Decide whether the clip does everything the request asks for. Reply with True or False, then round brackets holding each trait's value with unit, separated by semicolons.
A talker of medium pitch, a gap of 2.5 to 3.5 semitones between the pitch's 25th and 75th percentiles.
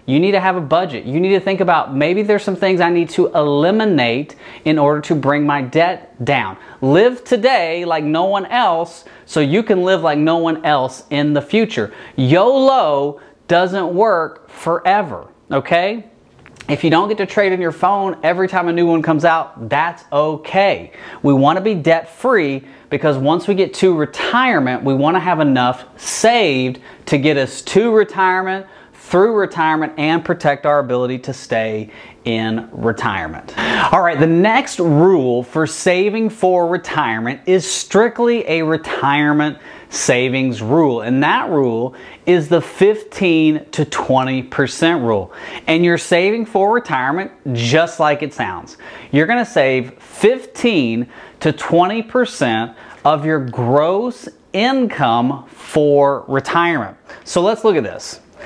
False (160 Hz; 5.3 semitones)